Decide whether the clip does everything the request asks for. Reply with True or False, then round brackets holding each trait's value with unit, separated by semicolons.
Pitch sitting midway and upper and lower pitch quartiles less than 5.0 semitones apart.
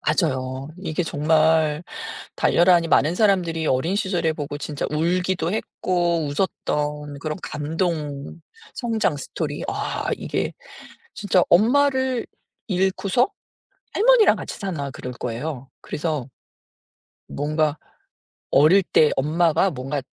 True (160 Hz; 4.2 semitones)